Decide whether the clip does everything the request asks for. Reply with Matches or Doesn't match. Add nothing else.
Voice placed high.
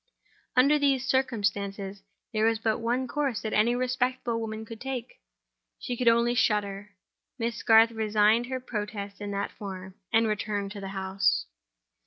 Matches